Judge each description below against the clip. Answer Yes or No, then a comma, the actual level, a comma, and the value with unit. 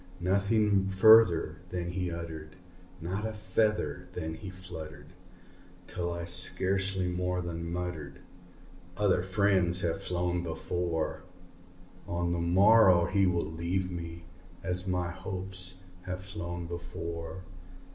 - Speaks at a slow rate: Yes, slow, 115 wpm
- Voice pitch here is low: Yes, very low, 90 Hz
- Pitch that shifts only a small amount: Yes, narrow, 1.8 semitones